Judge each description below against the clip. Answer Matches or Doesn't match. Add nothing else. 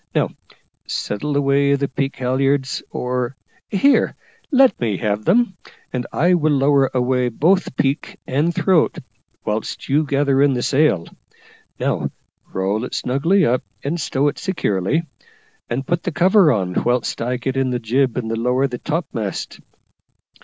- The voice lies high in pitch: Doesn't match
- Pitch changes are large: Doesn't match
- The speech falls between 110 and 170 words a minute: Matches